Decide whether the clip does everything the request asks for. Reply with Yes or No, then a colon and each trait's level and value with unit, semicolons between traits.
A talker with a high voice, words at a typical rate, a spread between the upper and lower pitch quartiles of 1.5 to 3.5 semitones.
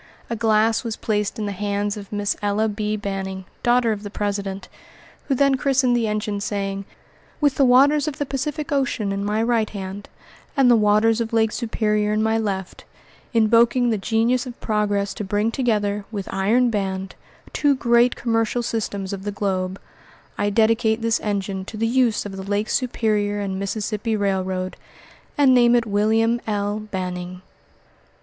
Yes: high, 215 Hz; average, 170 wpm; narrow, 2.6 semitones